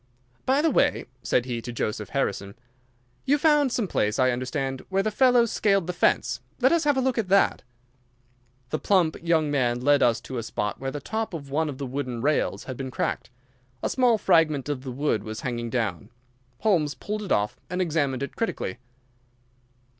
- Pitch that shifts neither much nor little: No, wide, 8.2 semitones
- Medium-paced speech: Yes, average, 195 wpm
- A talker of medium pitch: Yes, medium, 145 Hz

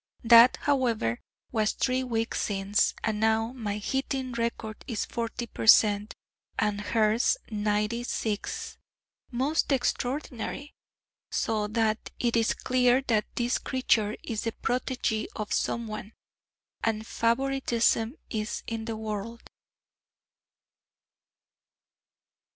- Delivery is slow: Yes, slow, 105 wpm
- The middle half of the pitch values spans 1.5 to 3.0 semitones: Yes, narrow, 2.5 semitones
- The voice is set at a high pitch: Yes, high, 230 Hz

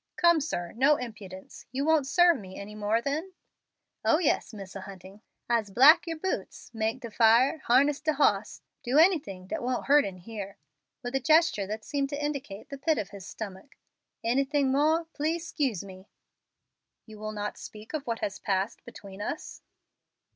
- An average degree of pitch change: No, wide, 6.2 semitones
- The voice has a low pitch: No, high, 240 Hz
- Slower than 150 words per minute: No, average, 175 wpm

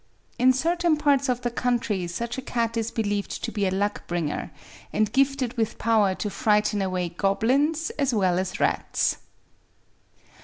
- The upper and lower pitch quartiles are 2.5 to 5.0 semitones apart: Yes, average, 4.6 semitones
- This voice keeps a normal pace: Yes, average, 160 wpm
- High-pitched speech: Yes, high, 225 Hz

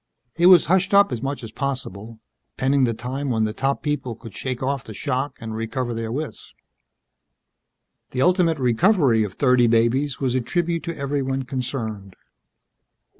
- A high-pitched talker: No, low, 130 Hz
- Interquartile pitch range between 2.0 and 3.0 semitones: No, average, 3.8 semitones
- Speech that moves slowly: No, average, 165 wpm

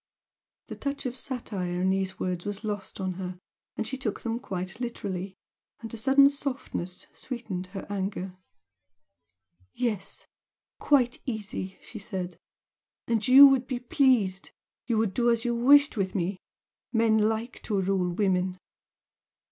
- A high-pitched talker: Yes, high, 215 Hz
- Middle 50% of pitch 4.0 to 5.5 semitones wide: Yes, average, 4.6 semitones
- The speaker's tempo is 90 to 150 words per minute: Yes, average, 140 wpm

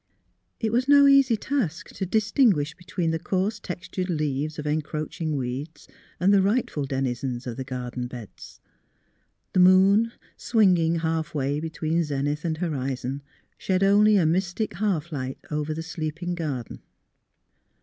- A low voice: No, medium, 160 Hz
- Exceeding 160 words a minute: No, average, 140 wpm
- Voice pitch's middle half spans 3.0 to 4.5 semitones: No, average, 4.9 semitones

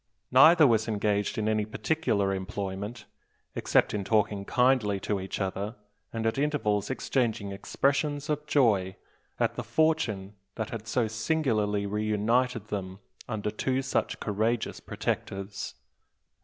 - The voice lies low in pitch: Yes, low, 110 Hz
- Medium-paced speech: No, slow, 130 wpm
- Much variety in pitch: No, average, 4.0 semitones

